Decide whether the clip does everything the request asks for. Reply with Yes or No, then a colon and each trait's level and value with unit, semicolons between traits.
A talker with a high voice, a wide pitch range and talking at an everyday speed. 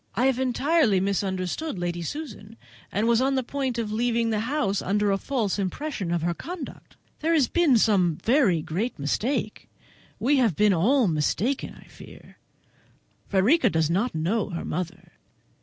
Yes: high, 220 Hz; wide, 6.1 semitones; average, 160 wpm